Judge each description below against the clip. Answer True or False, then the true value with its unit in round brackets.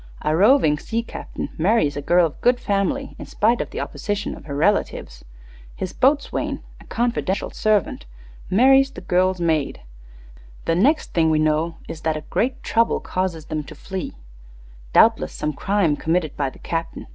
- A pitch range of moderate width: False (6.0 semitones)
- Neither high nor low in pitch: True (180 Hz)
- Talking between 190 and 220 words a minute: False (170 wpm)